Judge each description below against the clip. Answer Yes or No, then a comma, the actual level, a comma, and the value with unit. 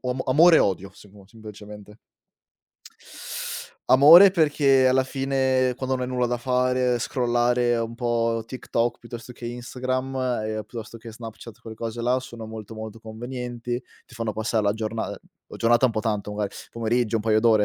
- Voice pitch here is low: Yes, low, 120 Hz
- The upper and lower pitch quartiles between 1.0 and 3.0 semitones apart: Yes, narrow, 2.5 semitones